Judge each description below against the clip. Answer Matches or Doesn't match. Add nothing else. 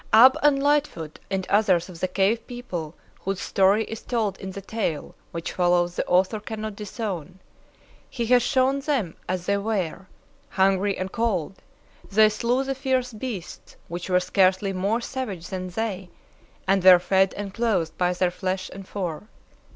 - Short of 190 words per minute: Matches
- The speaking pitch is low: Doesn't match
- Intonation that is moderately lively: Matches